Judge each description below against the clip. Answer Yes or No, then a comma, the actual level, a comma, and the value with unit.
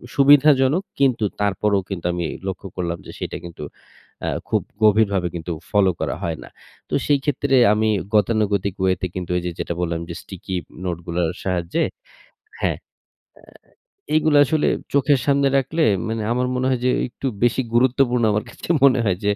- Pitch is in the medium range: No, low, 110 Hz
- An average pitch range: No, wide, 6.7 semitones